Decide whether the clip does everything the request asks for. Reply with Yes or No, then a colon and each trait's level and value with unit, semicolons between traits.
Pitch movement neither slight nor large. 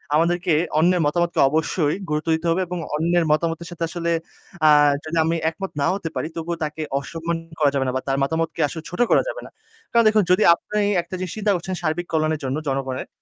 No: narrow, 2.2 semitones